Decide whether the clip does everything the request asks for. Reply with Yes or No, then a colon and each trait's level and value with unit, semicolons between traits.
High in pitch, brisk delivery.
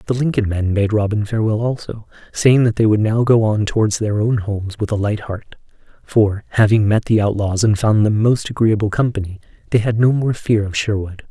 No: low, 110 Hz; fast, 210 wpm